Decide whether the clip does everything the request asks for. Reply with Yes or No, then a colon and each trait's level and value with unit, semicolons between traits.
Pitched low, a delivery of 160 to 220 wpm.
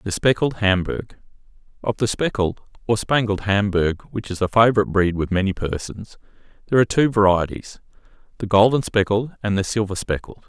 No: low, 105 Hz; average, 150 wpm